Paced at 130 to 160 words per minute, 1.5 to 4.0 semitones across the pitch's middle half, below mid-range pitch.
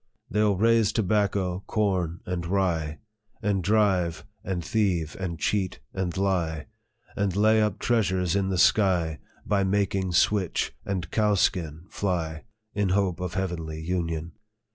Yes: average, 140 wpm; average, 3.0 semitones; very low, 95 Hz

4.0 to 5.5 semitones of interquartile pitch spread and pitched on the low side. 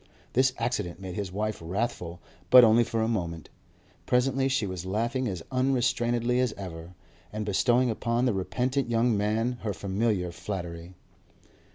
Yes: average, 4.6 semitones; low, 110 Hz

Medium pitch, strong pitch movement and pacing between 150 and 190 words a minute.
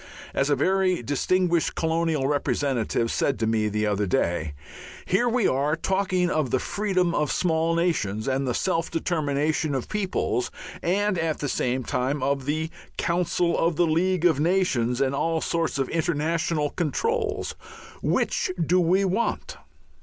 No: medium, 160 Hz; average, 4.7 semitones; average, 155 wpm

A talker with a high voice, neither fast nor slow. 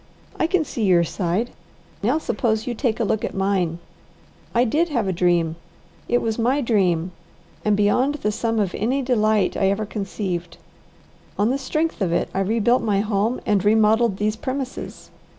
Yes: high, 215 Hz; average, 175 wpm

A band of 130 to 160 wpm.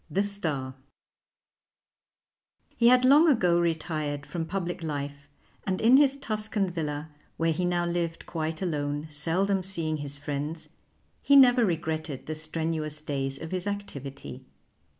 Yes: slow, 135 wpm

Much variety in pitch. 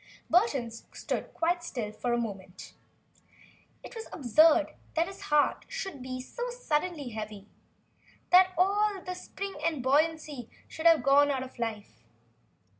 Yes: wide, 6.9 semitones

